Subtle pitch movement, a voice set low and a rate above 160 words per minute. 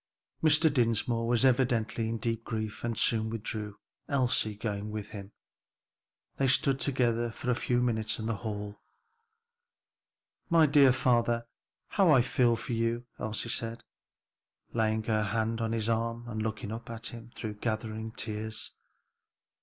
No: narrow, 1.8 semitones; low, 115 Hz; average, 145 wpm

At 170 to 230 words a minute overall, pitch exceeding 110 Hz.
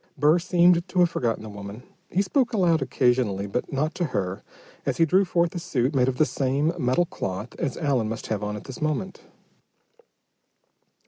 Yes: average, 190 wpm; medium, 140 Hz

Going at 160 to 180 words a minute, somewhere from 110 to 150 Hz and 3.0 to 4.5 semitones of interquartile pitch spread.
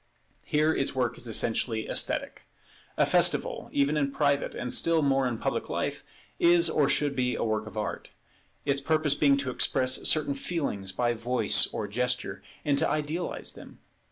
Yes: average, 170 wpm; medium, 140 Hz; average, 3.4 semitones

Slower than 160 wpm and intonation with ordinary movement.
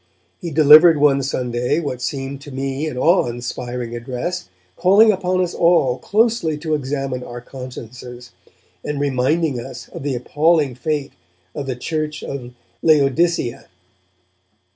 Yes: slow, 135 wpm; average, 4.2 semitones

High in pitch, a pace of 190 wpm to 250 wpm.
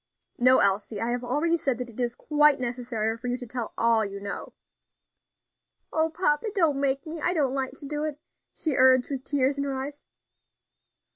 Yes: very high, 265 Hz; average, 195 wpm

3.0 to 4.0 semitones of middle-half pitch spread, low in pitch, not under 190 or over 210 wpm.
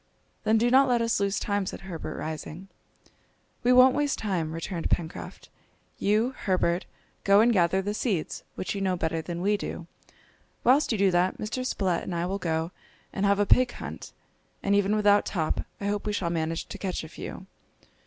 No: average, 3.7 semitones; high, 195 Hz; average, 195 wpm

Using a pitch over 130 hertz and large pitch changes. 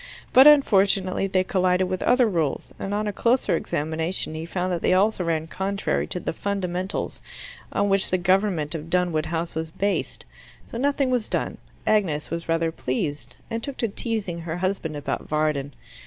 No: medium, 185 Hz; average, 3.8 semitones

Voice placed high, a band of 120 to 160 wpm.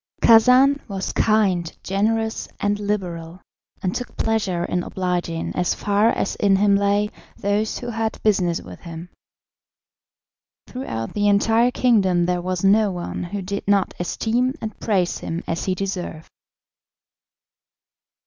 Yes: high, 200 Hz; slow, 135 wpm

